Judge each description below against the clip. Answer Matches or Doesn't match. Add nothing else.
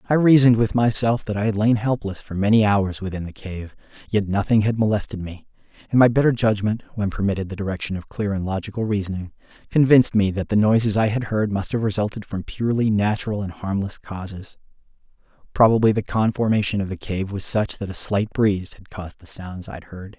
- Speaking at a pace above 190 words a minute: Matches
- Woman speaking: Doesn't match